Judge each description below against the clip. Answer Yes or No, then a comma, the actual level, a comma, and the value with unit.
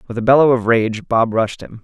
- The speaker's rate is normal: No, fast, 260 wpm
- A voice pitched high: No, low, 115 Hz